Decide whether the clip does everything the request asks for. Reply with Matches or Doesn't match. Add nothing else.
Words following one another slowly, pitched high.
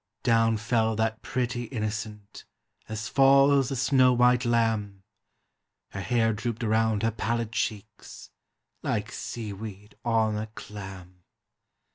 Doesn't match